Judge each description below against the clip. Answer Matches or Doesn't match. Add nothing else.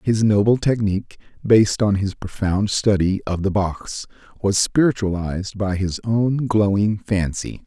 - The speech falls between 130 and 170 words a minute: Matches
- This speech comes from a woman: Doesn't match